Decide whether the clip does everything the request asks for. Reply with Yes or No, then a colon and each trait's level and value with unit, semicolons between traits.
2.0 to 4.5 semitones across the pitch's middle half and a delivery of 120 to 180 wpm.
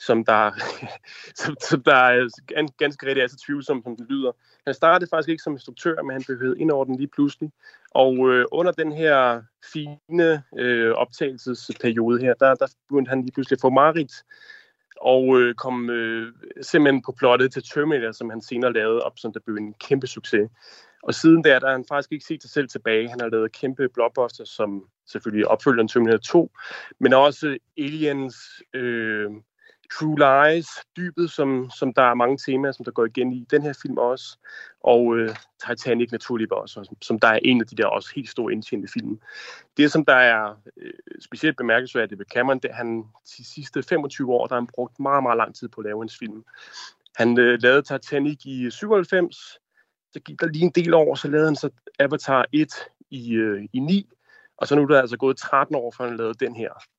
No: average, 3.6 semitones; average, 205 wpm